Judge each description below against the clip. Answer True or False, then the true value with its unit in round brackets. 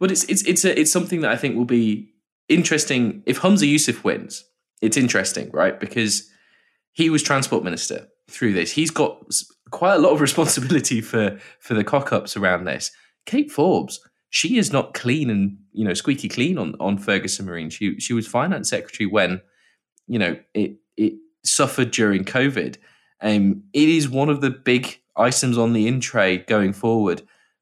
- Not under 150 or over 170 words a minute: False (180 wpm)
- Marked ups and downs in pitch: True (6.4 semitones)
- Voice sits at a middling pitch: False (125 Hz)